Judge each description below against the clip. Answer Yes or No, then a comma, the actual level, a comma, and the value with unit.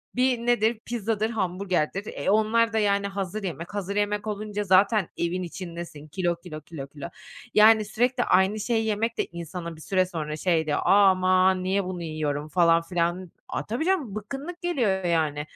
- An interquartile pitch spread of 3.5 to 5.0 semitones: Yes, average, 4.0 semitones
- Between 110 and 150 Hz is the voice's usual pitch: No, high, 190 Hz